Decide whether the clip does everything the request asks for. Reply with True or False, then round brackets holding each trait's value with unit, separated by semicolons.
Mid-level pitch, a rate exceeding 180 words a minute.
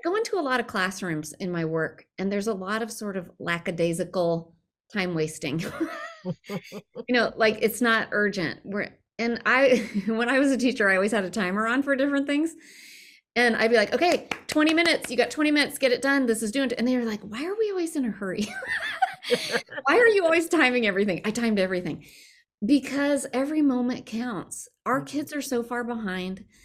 False (235 Hz; 200 wpm)